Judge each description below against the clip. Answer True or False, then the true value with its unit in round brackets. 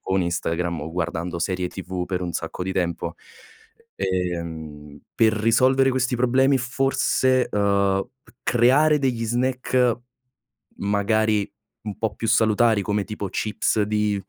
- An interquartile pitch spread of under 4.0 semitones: False (5.2 semitones)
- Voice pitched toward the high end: False (105 Hz)